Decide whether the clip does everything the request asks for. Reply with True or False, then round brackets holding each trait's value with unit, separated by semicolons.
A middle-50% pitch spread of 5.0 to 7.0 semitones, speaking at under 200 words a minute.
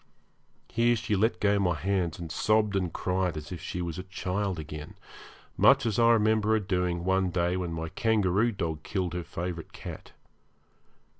False (3.3 semitones; 175 wpm)